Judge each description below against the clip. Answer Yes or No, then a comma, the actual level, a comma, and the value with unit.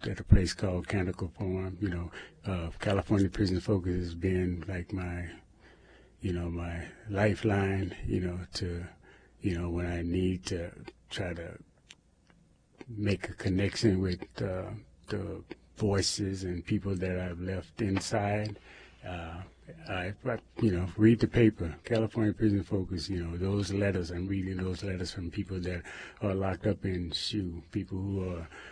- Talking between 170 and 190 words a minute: No, average, 155 wpm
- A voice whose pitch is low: Yes, very low, 95 Hz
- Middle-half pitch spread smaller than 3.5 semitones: Yes, narrow, 2.4 semitones